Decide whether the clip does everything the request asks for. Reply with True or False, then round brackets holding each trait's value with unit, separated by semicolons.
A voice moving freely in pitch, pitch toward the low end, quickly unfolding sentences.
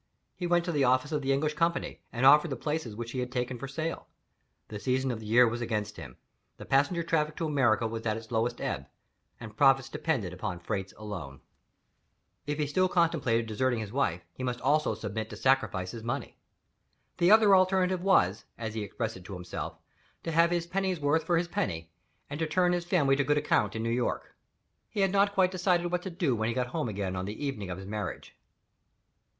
True (7.1 semitones; 130 Hz; 210 wpm)